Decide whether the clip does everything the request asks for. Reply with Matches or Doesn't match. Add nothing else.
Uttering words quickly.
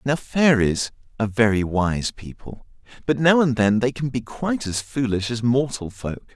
Doesn't match